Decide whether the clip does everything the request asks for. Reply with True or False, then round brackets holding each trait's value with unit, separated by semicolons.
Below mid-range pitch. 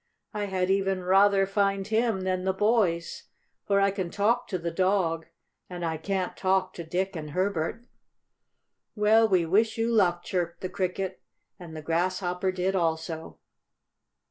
False (185 Hz)